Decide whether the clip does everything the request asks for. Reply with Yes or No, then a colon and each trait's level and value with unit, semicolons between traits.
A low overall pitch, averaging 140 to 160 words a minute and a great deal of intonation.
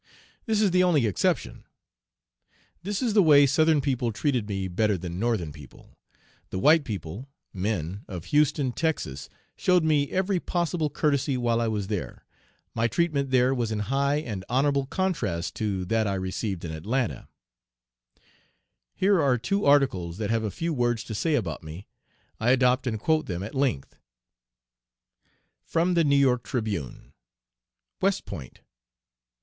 Yes: low, 125 Hz; average, 155 wpm; wide, 6.8 semitones